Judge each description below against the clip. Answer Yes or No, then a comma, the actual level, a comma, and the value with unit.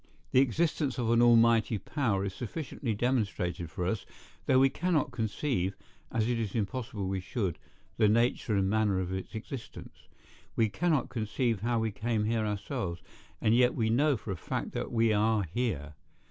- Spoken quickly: No, average, 175 wpm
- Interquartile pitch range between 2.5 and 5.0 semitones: Yes, average, 3.5 semitones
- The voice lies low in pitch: Yes, low, 110 Hz